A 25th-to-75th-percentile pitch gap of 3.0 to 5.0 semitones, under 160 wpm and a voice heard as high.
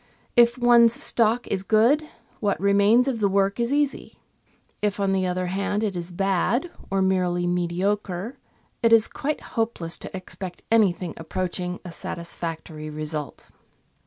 Yes: average, 4.3 semitones; average, 150 wpm; high, 195 Hz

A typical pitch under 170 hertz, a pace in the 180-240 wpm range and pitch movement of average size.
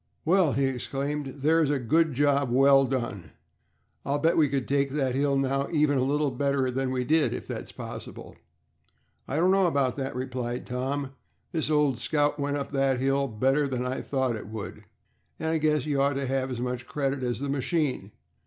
No: low, 135 Hz; average, 195 wpm; narrow, 2.1 semitones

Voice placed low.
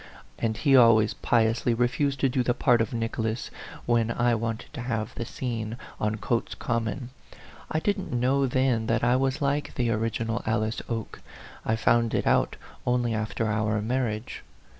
Yes: low, 115 Hz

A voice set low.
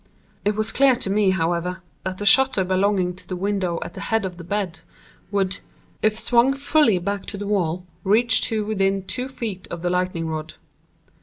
No: high, 195 Hz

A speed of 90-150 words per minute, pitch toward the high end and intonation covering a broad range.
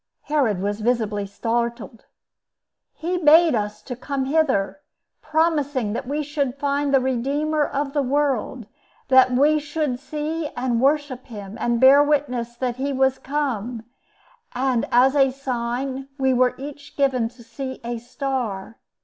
No: average, 140 wpm; very high, 265 Hz; average, 3.3 semitones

